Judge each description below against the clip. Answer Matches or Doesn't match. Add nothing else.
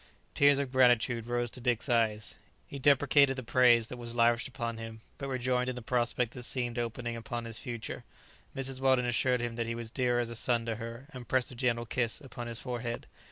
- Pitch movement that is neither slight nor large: Doesn't match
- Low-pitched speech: Matches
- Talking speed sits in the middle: Doesn't match